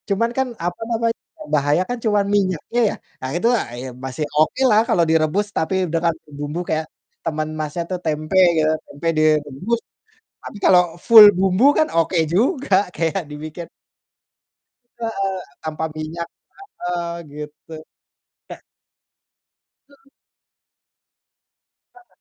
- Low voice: No, medium, 170 Hz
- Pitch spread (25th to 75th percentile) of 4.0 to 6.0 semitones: Yes, average, 4.9 semitones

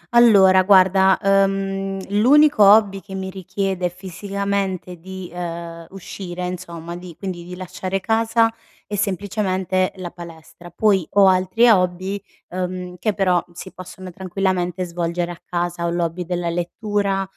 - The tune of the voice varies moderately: No, narrow, 1.8 semitones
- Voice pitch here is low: No, medium, 185 Hz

